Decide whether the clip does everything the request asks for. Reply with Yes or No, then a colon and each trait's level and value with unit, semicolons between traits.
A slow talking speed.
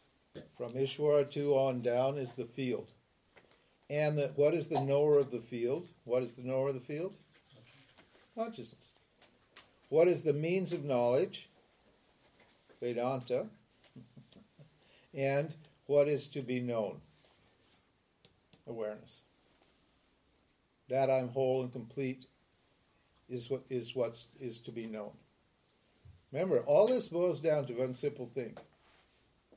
Yes: slow, 125 wpm